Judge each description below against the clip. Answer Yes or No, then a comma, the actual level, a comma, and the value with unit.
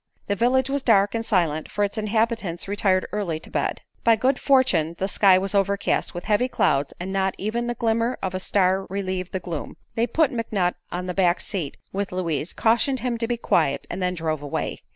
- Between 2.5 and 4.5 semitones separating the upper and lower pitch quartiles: Yes, average, 4.1 semitones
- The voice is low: No, high, 195 Hz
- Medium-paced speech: No, fast, 210 wpm